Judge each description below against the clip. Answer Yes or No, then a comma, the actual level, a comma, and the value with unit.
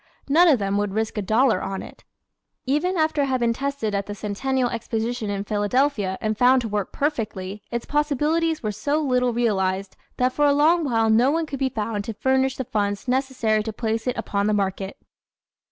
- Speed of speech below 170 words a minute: No, average, 200 wpm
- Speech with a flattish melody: No, average, 4.8 semitones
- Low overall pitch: No, high, 235 Hz